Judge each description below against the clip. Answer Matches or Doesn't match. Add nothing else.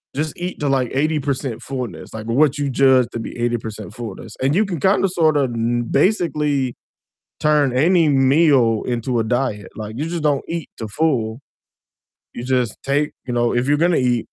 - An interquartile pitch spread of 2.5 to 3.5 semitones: Doesn't match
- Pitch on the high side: Doesn't match